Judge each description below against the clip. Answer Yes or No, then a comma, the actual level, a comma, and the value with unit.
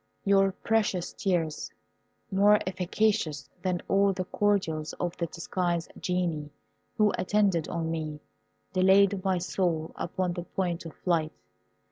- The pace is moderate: No, slow, 125 wpm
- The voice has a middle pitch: Yes, medium, 180 Hz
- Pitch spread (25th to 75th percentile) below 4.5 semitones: Yes, average, 2.7 semitones